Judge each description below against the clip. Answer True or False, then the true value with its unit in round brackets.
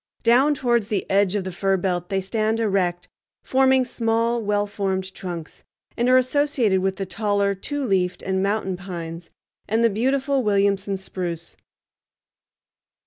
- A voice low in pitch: False (200 Hz)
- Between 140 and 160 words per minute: True (145 wpm)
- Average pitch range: True (3.7 semitones)